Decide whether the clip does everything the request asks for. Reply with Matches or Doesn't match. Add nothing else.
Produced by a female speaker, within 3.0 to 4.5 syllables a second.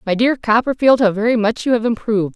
Doesn't match